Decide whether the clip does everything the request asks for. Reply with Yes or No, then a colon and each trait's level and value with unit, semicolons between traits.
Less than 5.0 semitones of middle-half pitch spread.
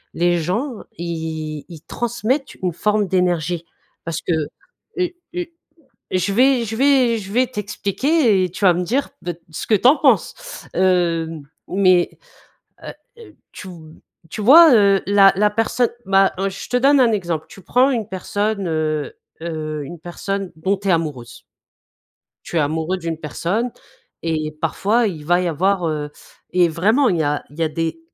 No: average, 5.3 semitones